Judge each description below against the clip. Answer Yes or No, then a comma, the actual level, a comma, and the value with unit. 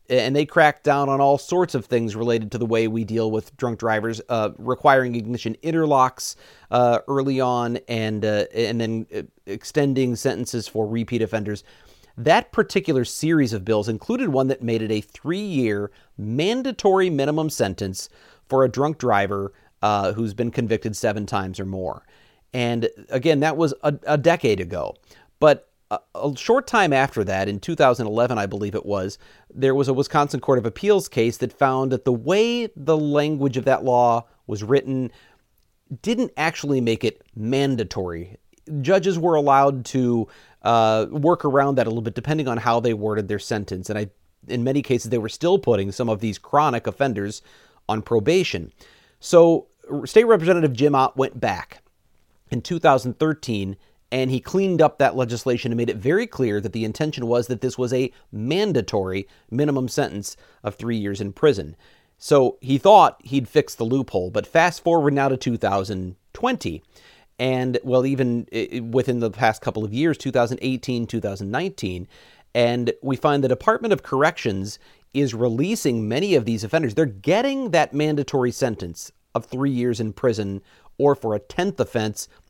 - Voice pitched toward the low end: Yes, low, 125 Hz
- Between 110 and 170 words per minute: Yes, average, 165 wpm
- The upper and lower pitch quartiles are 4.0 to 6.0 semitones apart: Yes, average, 4.3 semitones